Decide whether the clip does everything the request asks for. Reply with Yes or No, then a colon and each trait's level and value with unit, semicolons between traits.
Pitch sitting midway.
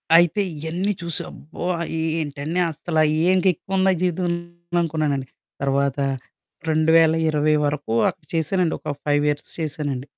Yes: medium, 155 Hz